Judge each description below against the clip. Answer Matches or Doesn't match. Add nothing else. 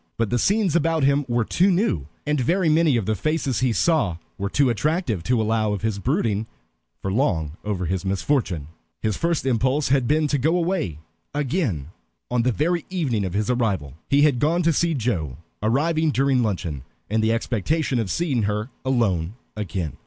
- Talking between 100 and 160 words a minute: Doesn't match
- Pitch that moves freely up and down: Matches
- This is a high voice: Doesn't match